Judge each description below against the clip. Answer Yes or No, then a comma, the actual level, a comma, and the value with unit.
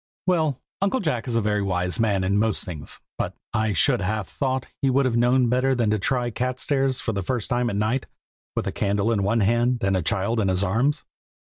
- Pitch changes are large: No, average, 4.3 semitones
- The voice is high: No, low, 115 Hz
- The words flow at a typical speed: No, fast, 235 wpm